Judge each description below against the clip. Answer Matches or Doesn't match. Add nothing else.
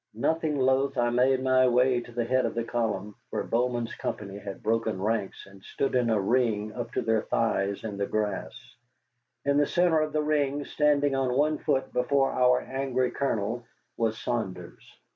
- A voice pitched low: Matches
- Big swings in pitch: Doesn't match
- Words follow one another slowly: Doesn't match